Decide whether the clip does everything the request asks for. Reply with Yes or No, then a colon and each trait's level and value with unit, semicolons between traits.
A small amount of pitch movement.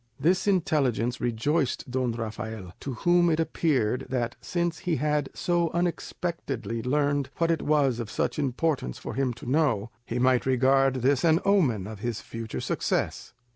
No: average, 5.2 semitones